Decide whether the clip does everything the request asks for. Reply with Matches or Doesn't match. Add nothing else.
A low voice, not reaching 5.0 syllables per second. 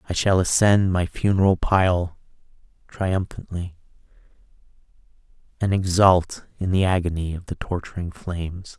Matches